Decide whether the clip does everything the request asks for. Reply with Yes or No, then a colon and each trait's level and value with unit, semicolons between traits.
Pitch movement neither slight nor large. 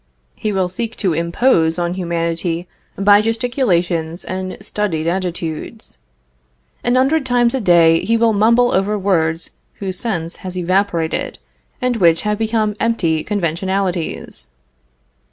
Yes: average, 4.8 semitones